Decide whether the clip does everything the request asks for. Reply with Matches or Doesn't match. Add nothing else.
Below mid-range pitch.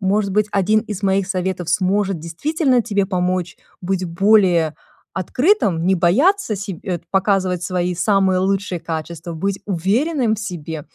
Doesn't match